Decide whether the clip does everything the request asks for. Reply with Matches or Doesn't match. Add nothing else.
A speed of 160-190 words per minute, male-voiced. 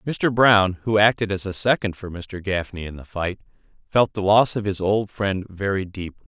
Doesn't match